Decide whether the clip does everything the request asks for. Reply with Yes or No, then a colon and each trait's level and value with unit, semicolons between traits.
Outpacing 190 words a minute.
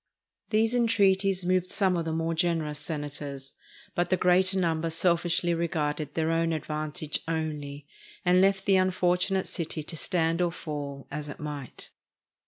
No: average, 150 wpm